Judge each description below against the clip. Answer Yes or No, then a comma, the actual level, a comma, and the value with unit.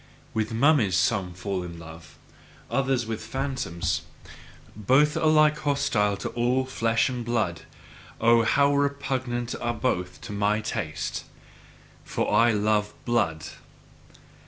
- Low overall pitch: Yes, low, 115 Hz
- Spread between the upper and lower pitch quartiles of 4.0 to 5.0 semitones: Yes, average, 4.7 semitones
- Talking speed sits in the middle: No, slow, 120 wpm